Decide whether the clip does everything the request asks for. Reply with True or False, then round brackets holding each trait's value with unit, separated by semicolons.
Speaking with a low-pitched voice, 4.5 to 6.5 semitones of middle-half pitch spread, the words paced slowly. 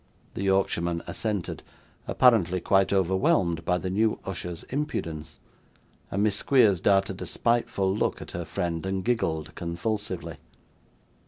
False (95 Hz; 3.2 semitones; 130 wpm)